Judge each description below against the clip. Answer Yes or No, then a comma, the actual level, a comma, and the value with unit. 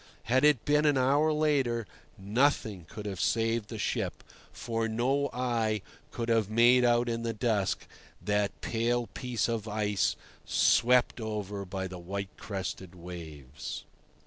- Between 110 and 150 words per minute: Yes, average, 145 wpm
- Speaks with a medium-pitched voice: No, low, 115 Hz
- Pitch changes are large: No, average, 3.4 semitones